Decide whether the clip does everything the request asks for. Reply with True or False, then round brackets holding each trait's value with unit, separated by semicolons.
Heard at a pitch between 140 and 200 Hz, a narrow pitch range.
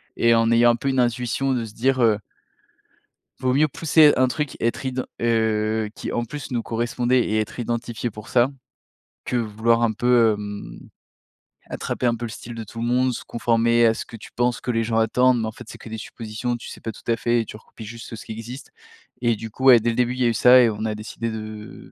False (115 Hz; 1.8 semitones)